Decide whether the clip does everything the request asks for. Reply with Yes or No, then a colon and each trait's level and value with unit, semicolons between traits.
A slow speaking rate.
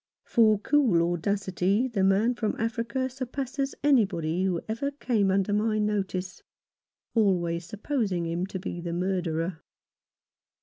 Yes: slow, 130 wpm